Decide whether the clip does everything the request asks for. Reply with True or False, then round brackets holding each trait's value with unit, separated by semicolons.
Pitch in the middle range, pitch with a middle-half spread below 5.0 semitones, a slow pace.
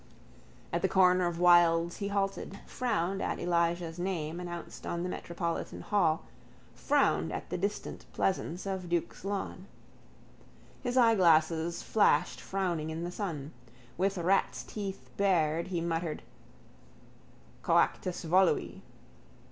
True (175 Hz; 2.6 semitones; 120 wpm)